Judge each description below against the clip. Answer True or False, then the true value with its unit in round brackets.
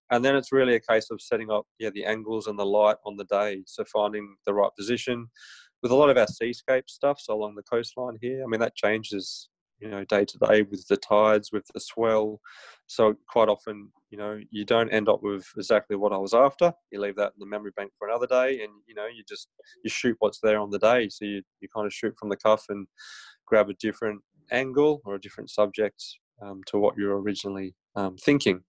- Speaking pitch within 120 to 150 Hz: False (105 Hz)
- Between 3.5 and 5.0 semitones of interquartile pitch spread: False (2.4 semitones)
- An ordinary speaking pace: False (235 wpm)